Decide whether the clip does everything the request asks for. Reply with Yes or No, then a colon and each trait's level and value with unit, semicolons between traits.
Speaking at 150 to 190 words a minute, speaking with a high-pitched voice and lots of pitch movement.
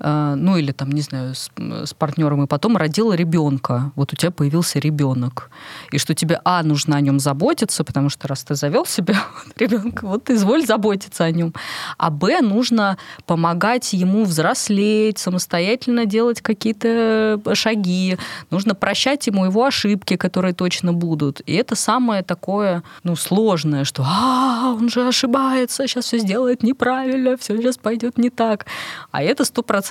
Yes: fast, 160 wpm; high, 195 Hz; wide, 6.3 semitones